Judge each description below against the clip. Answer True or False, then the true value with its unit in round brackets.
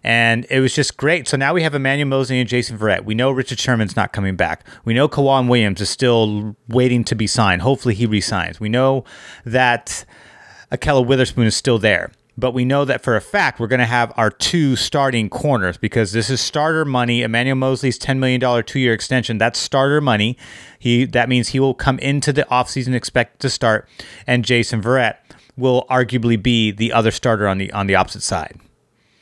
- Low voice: True (125 Hz)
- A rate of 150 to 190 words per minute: False (205 wpm)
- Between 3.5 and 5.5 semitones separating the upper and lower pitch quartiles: False (2.8 semitones)